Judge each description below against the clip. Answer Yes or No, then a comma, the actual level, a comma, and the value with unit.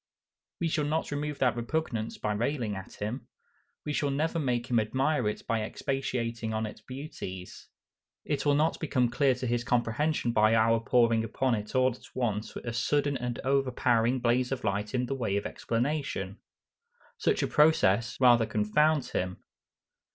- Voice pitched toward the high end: No, low, 120 Hz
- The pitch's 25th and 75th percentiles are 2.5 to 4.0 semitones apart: Yes, average, 3.7 semitones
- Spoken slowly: No, average, 165 wpm